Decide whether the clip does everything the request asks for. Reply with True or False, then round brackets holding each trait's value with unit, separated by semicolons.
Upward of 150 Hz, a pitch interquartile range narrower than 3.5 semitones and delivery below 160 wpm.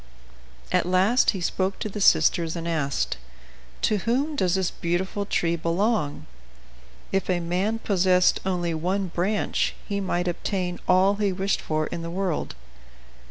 True (185 Hz; 2.6 semitones; 150 wpm)